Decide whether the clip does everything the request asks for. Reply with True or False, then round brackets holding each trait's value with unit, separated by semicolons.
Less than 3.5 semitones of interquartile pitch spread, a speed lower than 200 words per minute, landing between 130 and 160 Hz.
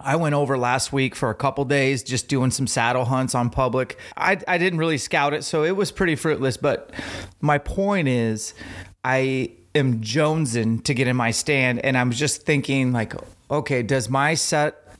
True (3.1 semitones; 190 wpm; 135 Hz)